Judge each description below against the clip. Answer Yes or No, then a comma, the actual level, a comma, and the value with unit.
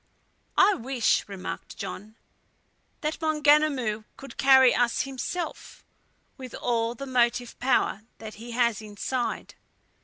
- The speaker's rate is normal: No, slow, 115 wpm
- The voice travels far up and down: No, average, 3.1 semitones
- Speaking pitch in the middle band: No, high, 245 Hz